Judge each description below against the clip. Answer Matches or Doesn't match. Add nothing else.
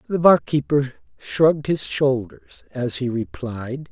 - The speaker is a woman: Doesn't match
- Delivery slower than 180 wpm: Matches